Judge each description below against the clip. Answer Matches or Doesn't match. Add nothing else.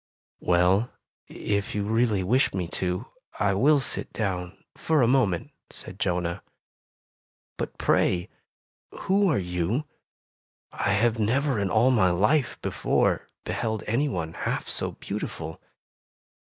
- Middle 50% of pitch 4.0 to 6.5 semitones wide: Matches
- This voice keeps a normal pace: Doesn't match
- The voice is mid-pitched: Doesn't match